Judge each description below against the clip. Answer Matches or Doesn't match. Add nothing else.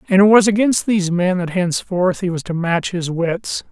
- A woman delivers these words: Doesn't match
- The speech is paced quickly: Matches